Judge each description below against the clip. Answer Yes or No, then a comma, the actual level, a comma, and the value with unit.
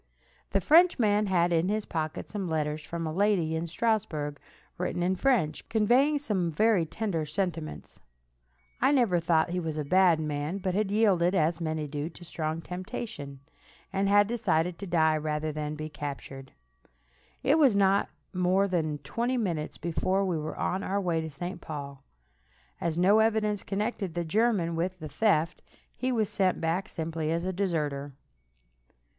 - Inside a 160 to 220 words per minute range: Yes, average, 165 wpm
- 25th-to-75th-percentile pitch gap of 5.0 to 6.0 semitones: No, average, 4.4 semitones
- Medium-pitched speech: Yes, medium, 175 Hz